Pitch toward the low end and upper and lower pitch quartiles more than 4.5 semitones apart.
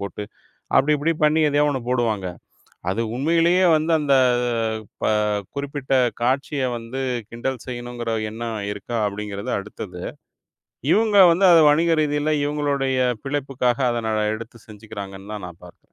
Yes: low, 130 Hz; average, 5.2 semitones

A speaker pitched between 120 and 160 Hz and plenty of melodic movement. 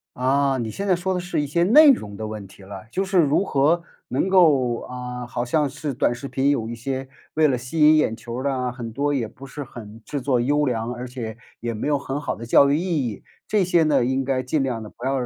No: low, 135 Hz; average, 3.9 semitones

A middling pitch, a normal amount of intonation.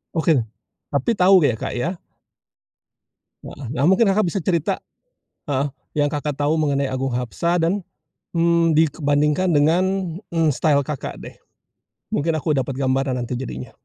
Yes: medium, 150 Hz; average, 3.9 semitones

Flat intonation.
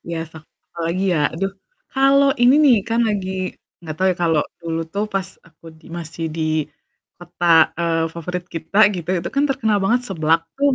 No: average, 4.6 semitones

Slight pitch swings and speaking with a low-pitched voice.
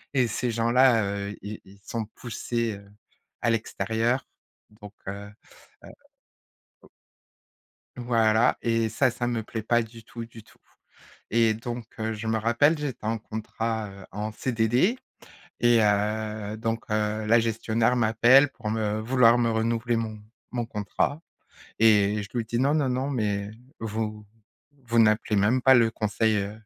Yes: narrow, 1.8 semitones; low, 115 Hz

